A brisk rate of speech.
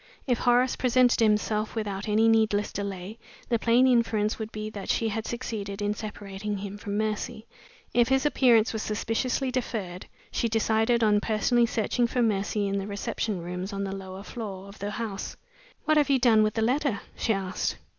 No: average, 185 wpm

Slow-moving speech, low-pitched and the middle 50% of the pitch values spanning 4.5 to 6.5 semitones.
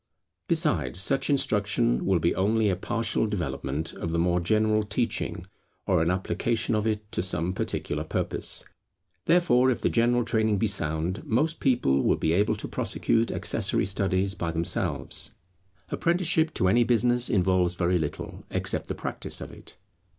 No: average, 160 wpm; low, 105 Hz; average, 4.9 semitones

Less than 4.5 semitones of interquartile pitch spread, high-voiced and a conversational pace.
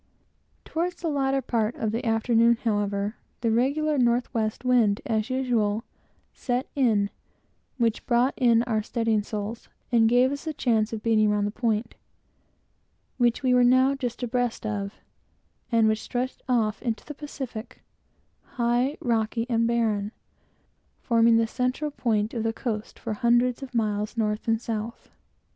Yes: narrow, 2.4 semitones; high, 235 Hz; average, 150 wpm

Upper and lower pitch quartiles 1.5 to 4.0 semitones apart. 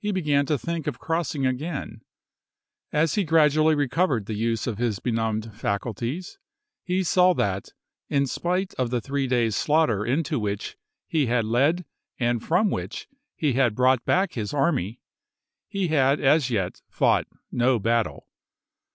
No: wide, 5.6 semitones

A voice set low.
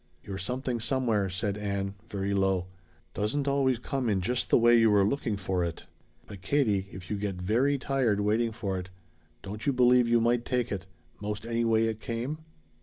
Yes: low, 110 Hz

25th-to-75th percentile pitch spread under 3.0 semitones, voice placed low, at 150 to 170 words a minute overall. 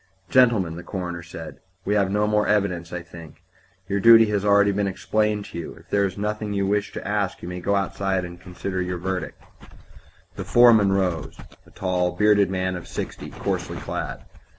No: narrow, 2.6 semitones; very low, 95 Hz; average, 190 wpm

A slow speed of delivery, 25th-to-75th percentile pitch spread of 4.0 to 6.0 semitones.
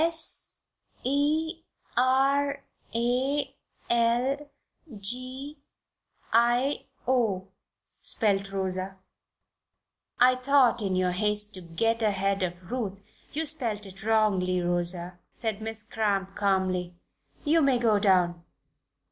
Yes: slow, 105 wpm; average, 5.2 semitones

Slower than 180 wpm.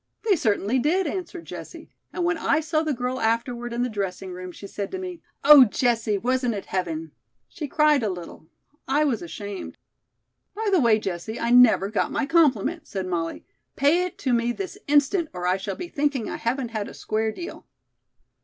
No: average, 195 wpm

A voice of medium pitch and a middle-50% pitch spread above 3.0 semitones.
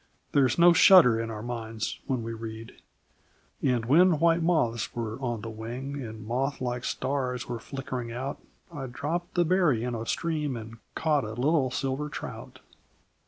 No: low, 125 Hz; average, 4.4 semitones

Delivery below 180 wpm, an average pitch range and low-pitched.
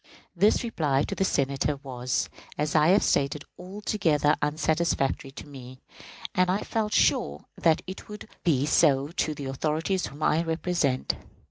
No: average, 150 wpm; average, 4.5 semitones; medium, 155 Hz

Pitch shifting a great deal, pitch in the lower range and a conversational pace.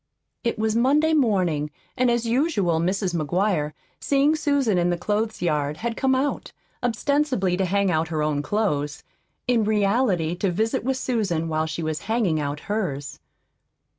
No: wide, 6.7 semitones; high, 200 Hz; average, 160 wpm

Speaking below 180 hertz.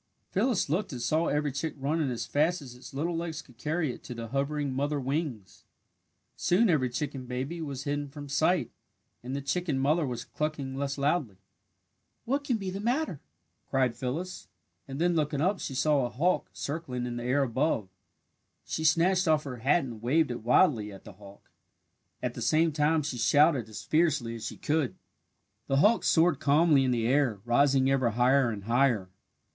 Yes: medium, 140 Hz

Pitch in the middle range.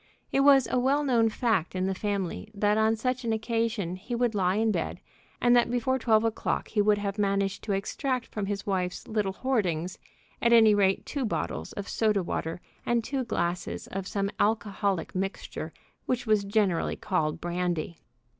No: high, 210 Hz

